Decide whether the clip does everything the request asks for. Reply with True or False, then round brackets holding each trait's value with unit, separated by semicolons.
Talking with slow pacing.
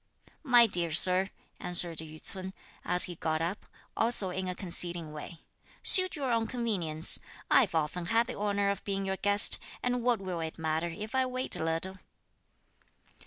False (170 wpm)